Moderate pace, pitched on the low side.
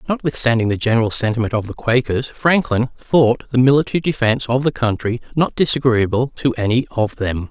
Yes: average, 170 wpm; low, 125 Hz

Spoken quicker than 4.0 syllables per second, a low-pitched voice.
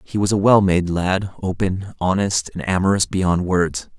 Yes: 4.5 syllables/s; very low, 95 Hz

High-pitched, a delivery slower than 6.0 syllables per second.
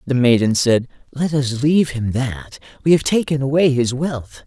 No: low, 130 Hz; 4.7 syllables/s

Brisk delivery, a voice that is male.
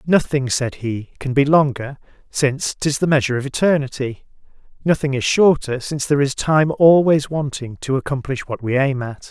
No: average, 175 wpm; male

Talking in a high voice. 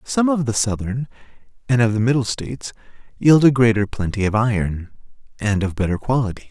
No: low, 115 Hz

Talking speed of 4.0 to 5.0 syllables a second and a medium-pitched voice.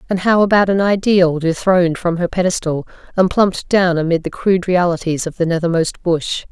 No: 5.5 syllables/s; medium, 175 Hz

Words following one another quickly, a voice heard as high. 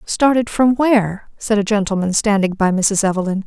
No: average, 175 wpm; high, 210 Hz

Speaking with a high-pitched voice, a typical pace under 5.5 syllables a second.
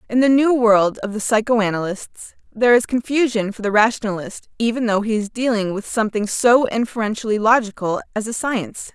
No: high, 225 Hz; 5.7 syllables/s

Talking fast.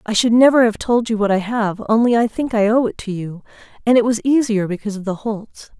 Yes: fast, 260 wpm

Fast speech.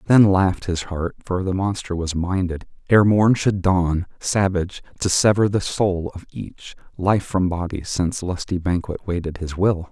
No: average, 175 wpm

